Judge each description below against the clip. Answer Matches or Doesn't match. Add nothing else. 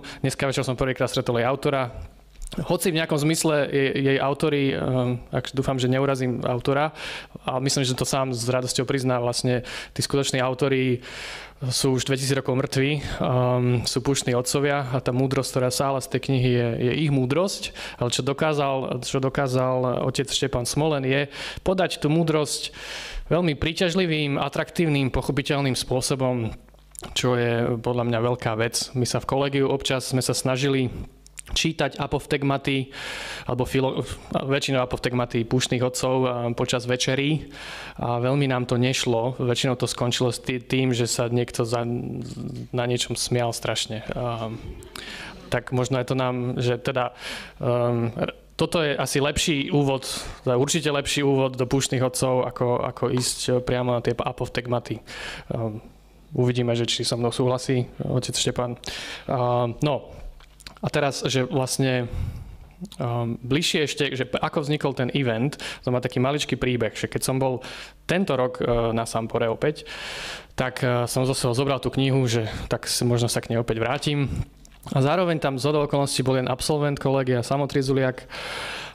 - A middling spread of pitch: Doesn't match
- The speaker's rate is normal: Matches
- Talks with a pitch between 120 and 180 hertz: Matches